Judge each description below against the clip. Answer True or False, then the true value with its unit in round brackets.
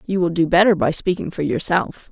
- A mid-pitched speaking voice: True (170 Hz)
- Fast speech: True (225 wpm)